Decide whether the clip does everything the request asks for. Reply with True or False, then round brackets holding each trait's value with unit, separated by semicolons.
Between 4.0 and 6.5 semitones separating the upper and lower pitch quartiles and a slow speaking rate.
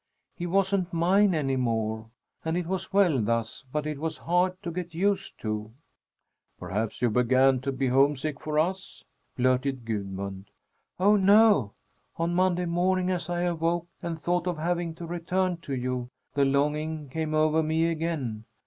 False (5.4 semitones; 160 wpm)